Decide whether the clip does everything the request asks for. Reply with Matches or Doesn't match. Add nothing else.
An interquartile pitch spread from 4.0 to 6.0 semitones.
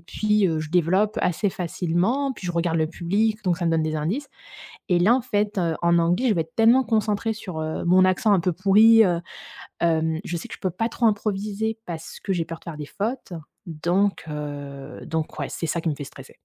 Matches